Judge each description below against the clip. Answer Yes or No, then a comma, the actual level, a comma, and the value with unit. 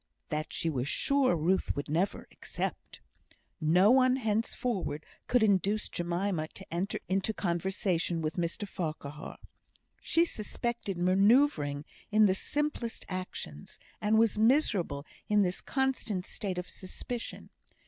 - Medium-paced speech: No, slow, 125 wpm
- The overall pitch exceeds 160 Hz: Yes, high, 190 Hz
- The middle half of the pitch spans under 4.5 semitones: No, average, 4.8 semitones